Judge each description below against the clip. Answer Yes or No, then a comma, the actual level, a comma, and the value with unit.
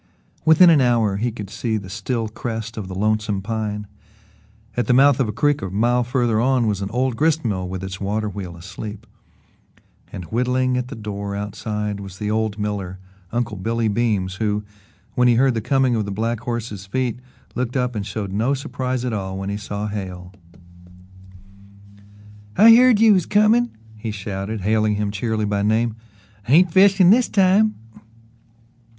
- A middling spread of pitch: Yes, average, 3.7 semitones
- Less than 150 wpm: No, average, 175 wpm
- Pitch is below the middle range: Yes, low, 110 Hz